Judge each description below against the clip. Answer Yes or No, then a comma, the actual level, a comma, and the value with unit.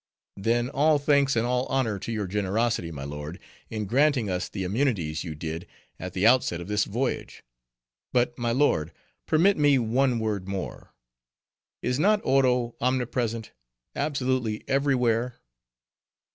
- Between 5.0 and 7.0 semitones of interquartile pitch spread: Yes, average, 5.3 semitones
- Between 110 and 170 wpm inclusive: Yes, average, 140 wpm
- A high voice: No, low, 115 Hz